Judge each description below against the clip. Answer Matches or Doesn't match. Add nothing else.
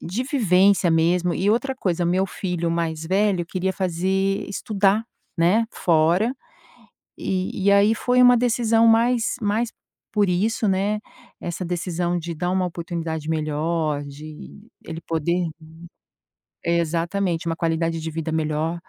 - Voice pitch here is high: Doesn't match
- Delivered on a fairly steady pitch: Doesn't match